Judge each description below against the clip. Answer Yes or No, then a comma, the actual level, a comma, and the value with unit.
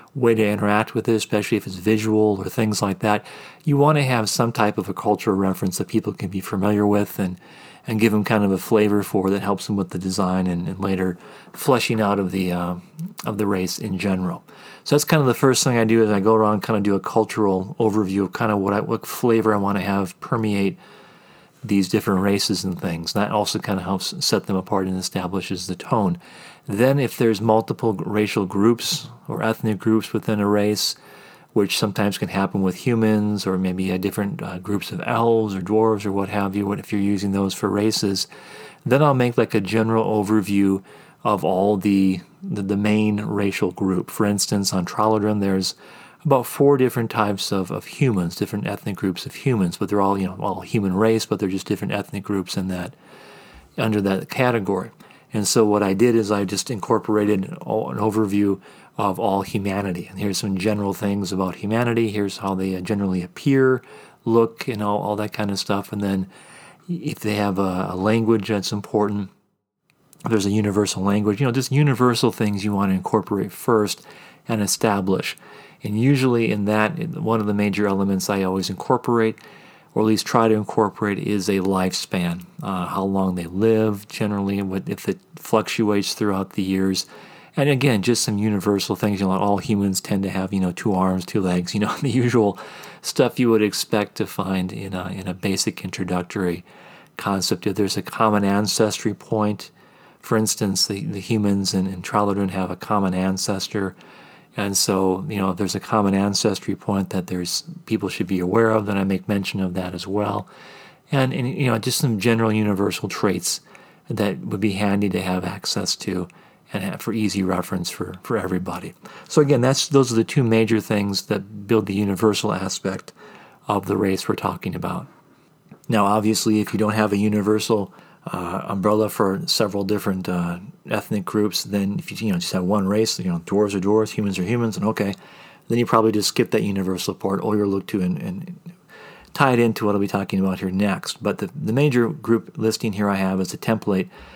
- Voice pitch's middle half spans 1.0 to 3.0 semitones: Yes, narrow, 2.4 semitones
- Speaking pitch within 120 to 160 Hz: No, low, 105 Hz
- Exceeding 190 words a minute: Yes, average, 200 wpm